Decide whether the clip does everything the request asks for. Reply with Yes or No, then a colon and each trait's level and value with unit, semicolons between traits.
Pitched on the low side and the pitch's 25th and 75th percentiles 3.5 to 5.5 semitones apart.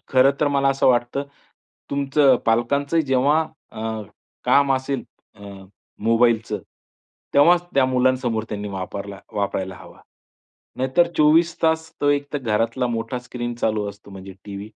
Yes: low, 125 Hz; average, 4.3 semitones